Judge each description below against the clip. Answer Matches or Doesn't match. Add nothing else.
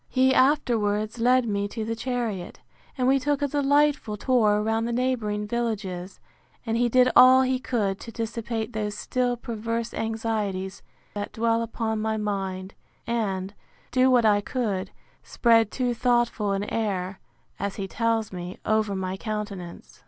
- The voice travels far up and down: Doesn't match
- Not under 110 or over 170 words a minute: Matches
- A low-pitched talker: Doesn't match